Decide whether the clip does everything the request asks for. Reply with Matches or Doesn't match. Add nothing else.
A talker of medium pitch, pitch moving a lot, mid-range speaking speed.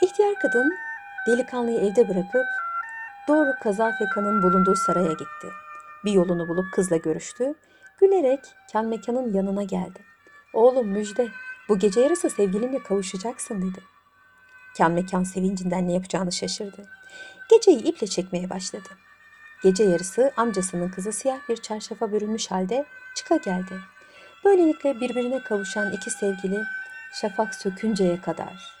Doesn't match